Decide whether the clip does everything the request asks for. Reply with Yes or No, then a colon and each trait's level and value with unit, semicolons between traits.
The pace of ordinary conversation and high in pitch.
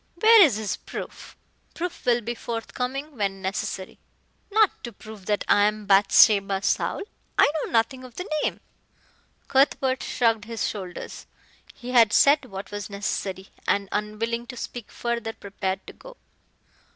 Yes: average, 150 wpm; high, 225 Hz